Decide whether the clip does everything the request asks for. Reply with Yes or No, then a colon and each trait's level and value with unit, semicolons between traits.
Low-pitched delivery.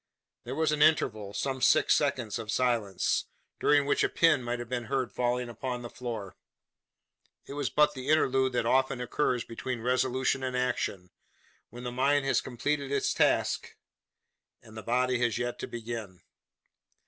Yes: low, 125 Hz